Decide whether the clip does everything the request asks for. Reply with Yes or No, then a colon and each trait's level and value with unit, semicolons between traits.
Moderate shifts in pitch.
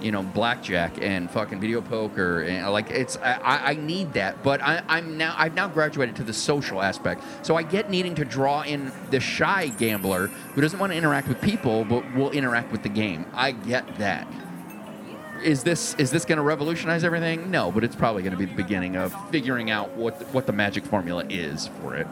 No: wide, 6.6 semitones